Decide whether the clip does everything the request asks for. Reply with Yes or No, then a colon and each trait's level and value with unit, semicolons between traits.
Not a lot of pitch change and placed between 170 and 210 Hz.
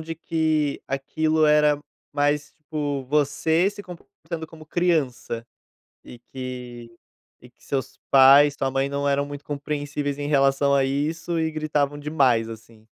No: narrow, 2.3 semitones; medium, 145 Hz